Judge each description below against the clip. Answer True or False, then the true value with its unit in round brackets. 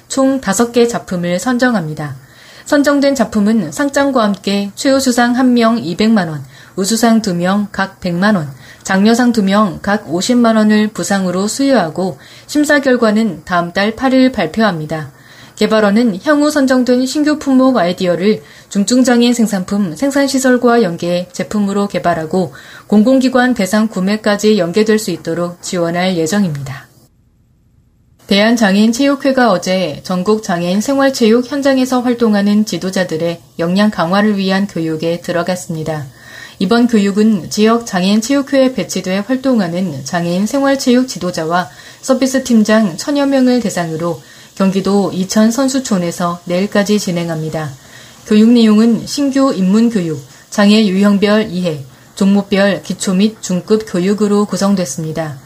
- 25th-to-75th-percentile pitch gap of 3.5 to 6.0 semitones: True (5.1 semitones)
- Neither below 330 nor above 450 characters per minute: False (305 characters per minute)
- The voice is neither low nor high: False (200 Hz)